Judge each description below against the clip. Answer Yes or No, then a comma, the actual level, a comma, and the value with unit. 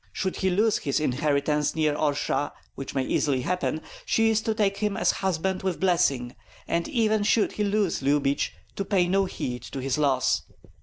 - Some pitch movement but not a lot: No, wide, 5.8 semitones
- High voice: No, medium, 175 Hz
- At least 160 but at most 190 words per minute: Yes, average, 185 wpm